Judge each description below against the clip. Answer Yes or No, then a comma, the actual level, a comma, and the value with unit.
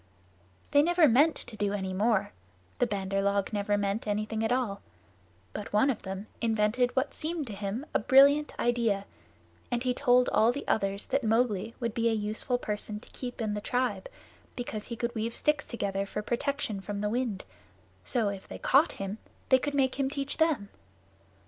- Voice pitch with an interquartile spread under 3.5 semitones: No, average, 3.8 semitones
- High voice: Yes, high, 225 Hz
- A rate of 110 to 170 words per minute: No, average, 185 wpm